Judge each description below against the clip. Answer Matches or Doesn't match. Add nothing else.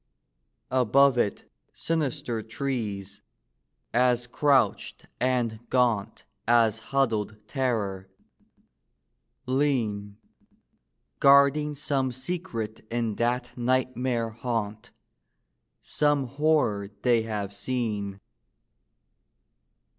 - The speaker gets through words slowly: Matches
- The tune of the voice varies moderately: Matches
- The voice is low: Matches